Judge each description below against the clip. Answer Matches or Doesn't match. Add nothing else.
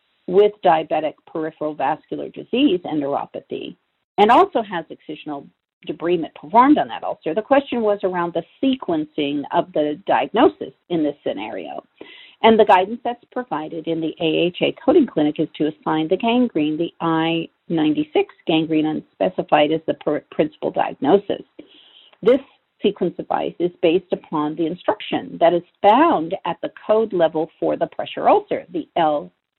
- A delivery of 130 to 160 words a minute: Matches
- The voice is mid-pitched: Matches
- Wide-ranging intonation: Matches